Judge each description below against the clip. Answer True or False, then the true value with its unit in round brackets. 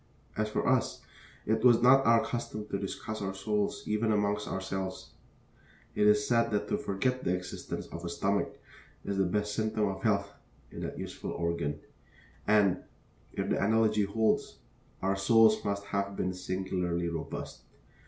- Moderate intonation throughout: False (2.2 semitones)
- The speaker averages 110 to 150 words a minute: False (160 wpm)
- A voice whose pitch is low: True (100 Hz)